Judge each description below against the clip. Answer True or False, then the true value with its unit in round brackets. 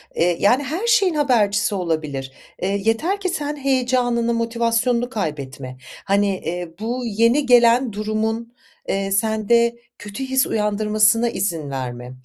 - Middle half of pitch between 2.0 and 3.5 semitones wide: False (3.9 semitones)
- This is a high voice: True (225 Hz)